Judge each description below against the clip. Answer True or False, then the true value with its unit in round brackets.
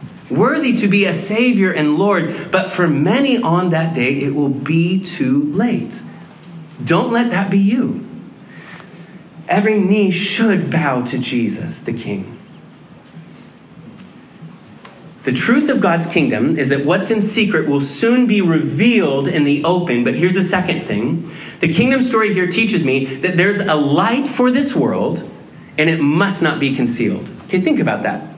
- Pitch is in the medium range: True (180 Hz)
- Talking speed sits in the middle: True (160 wpm)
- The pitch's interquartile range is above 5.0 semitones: True (5.6 semitones)